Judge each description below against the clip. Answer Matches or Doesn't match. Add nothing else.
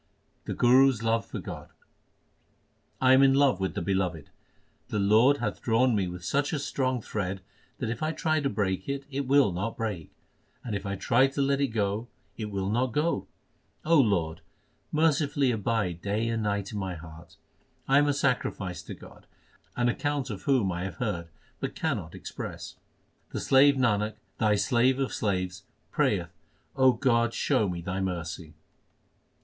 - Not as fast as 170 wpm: Doesn't match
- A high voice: Doesn't match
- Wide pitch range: Matches